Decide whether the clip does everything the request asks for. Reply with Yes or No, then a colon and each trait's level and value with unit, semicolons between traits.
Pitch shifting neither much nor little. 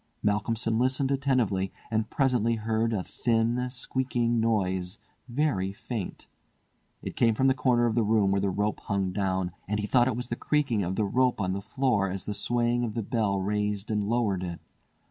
Yes: average, 3.5 semitones